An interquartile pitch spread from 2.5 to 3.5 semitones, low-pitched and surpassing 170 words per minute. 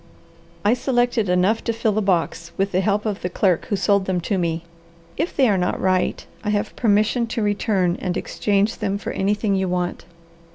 No: average, 2.9 semitones; high, 200 Hz; average, 200 wpm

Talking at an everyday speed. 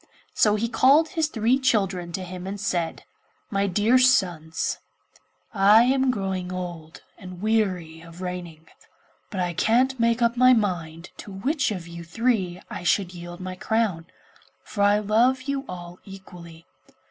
Yes: average, 160 wpm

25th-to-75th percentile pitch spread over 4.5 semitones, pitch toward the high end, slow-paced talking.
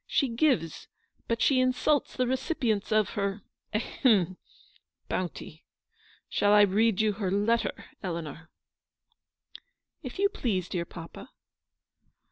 Yes: average, 5.2 semitones; high, 215 Hz; slow, 130 wpm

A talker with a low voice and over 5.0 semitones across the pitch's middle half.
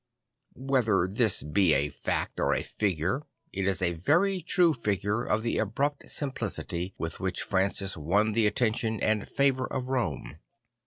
Yes: low, 105 Hz; wide, 5.4 semitones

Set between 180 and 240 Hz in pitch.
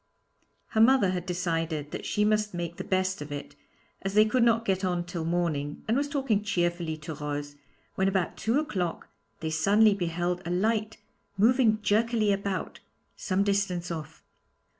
Yes: high, 190 Hz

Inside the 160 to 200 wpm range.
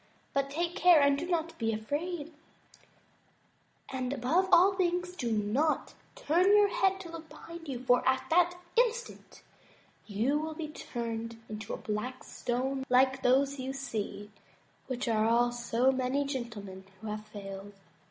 No: average, 150 wpm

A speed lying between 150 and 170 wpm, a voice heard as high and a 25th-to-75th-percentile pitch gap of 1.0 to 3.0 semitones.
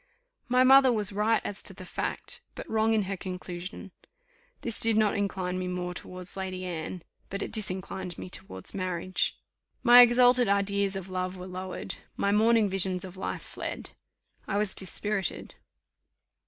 Yes: average, 160 wpm; high, 195 Hz; average, 2.7 semitones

